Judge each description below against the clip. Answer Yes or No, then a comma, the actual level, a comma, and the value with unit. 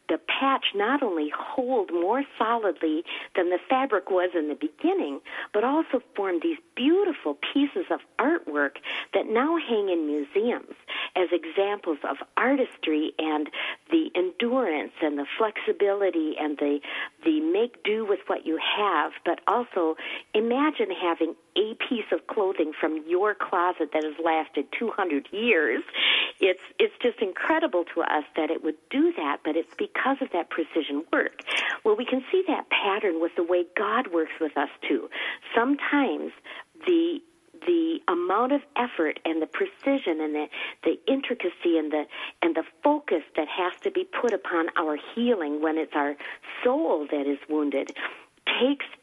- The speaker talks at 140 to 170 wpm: Yes, average, 160 wpm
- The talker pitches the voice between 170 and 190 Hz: No, high, 205 Hz